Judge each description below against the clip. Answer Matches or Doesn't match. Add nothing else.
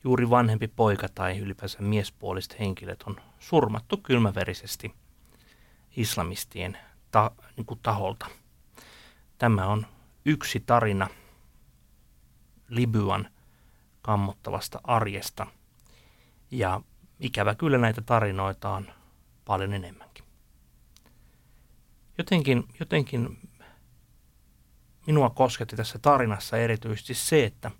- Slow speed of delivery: Matches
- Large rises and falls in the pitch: Doesn't match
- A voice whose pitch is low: Matches